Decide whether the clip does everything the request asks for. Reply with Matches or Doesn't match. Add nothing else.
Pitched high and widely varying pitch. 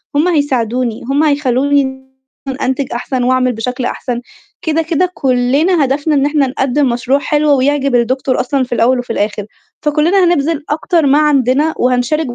Doesn't match